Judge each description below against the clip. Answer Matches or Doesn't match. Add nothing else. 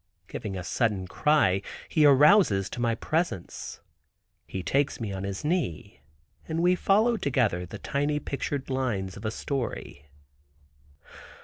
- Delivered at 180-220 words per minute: Doesn't match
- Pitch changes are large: Matches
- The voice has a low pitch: Matches